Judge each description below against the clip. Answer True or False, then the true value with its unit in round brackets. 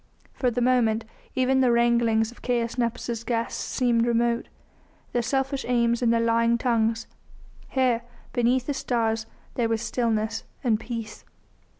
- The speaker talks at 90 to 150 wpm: True (140 wpm)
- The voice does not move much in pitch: True (1.4 semitones)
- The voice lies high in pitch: True (235 Hz)